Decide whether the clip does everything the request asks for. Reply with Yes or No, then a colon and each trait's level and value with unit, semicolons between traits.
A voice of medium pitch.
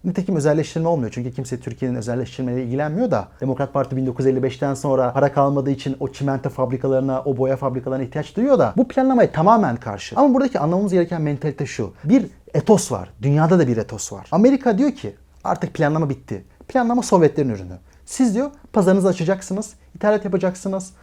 Yes: medium, 145 Hz